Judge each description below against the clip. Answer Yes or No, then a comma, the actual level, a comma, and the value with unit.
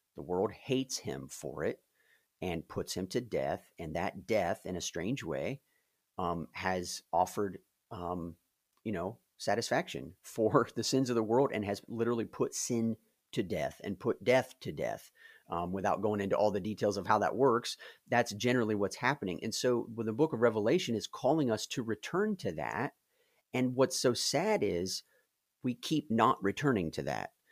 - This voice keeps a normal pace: Yes, average, 185 wpm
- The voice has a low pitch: Yes, low, 115 Hz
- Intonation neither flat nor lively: Yes, average, 4.1 semitones